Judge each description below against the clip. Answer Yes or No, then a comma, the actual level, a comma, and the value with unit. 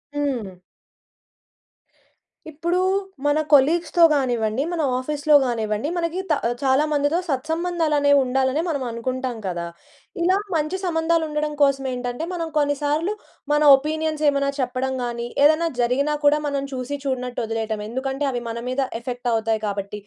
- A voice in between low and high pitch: No, very high, 280 Hz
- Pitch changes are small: No, average, 3.8 semitones